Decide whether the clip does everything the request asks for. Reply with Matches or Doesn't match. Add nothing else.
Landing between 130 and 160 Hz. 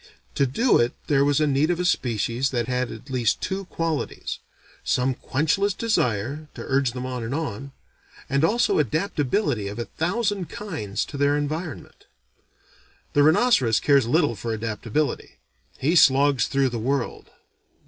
Matches